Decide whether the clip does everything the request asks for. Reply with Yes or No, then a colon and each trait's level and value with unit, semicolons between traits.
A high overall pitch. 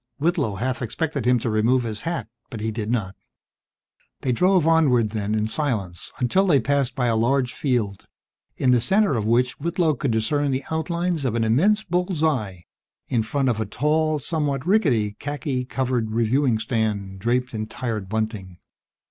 No: low, 125 Hz